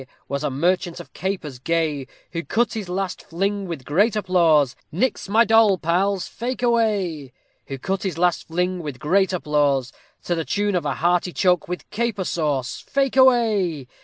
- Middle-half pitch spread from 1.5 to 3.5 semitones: No, average, 4.8 semitones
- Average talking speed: Yes, average, 175 wpm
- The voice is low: No, medium, 180 Hz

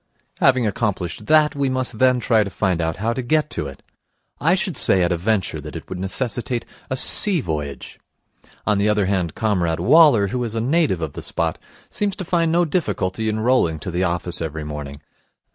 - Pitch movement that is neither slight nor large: No, wide, 6.9 semitones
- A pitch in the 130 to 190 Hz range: No, low, 110 Hz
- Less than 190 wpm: No, fast, 205 wpm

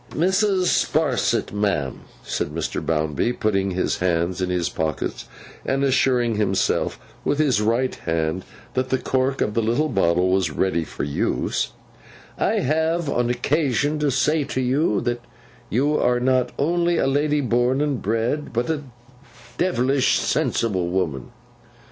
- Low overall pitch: Yes, low, 120 Hz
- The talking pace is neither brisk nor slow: Yes, average, 145 wpm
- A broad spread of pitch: Yes, wide, 7.2 semitones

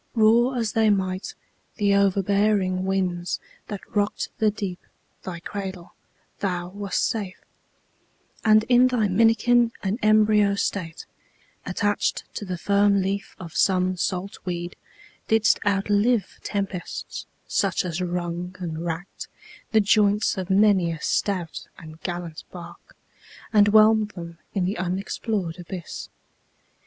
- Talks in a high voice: Yes, high, 195 Hz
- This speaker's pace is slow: Yes, slow, 125 wpm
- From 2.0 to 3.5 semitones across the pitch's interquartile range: Yes, average, 2.8 semitones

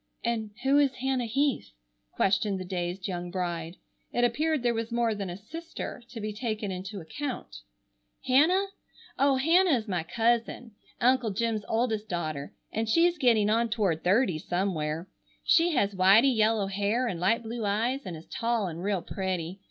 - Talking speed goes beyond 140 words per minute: Yes, average, 165 wpm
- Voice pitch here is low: No, high, 220 Hz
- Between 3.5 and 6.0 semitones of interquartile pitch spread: Yes, average, 4.8 semitones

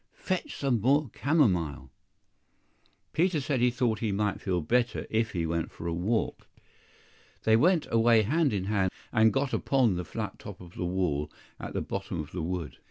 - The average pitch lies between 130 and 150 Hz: No, low, 110 Hz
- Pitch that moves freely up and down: Yes, wide, 6.2 semitones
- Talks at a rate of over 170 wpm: Yes, average, 180 wpm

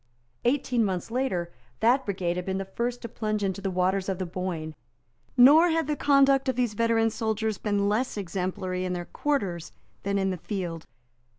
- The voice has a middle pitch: No, high, 205 Hz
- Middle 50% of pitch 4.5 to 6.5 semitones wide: Yes, average, 4.8 semitones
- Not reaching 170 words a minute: No, average, 185 wpm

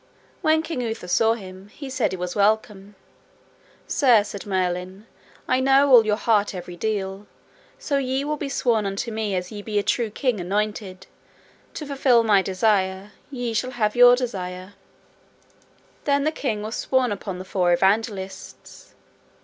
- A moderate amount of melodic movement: Yes, average, 4.5 semitones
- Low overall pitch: No, high, 215 Hz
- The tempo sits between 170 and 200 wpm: No, average, 160 wpm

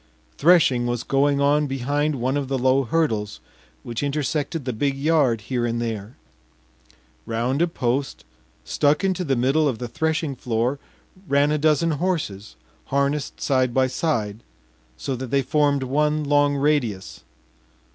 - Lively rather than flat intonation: No, average, 3.6 semitones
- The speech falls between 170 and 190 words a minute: No, average, 145 wpm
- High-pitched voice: No, medium, 140 Hz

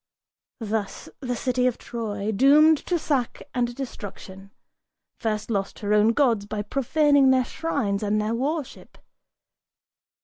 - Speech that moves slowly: Yes, slow, 130 wpm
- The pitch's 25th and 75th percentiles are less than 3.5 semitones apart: No, average, 4.6 semitones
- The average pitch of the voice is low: No, high, 235 Hz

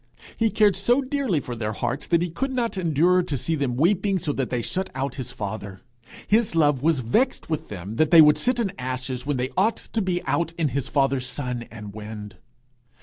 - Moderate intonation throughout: No, wide, 7.0 semitones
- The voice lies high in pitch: No, medium, 150 Hz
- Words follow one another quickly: Yes, fast, 215 wpm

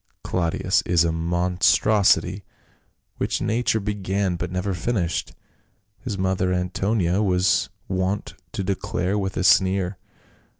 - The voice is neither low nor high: No, very low, 95 Hz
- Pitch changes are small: Yes, narrow, 2.0 semitones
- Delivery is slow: Yes, slow, 120 wpm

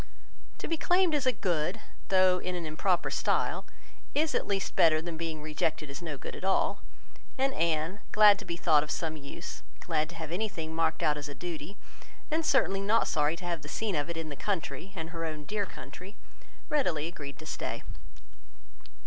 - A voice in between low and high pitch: Yes, medium, 170 Hz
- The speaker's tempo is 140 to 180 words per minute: No, average, 200 wpm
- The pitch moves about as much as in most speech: Yes, average, 4.0 semitones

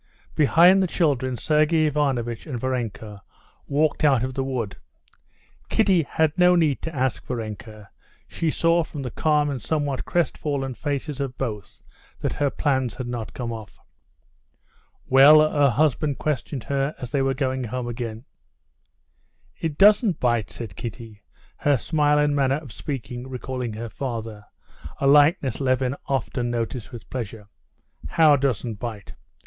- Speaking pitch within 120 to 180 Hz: Yes, low, 135 Hz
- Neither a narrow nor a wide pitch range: Yes, average, 3.9 semitones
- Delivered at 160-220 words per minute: No, average, 145 wpm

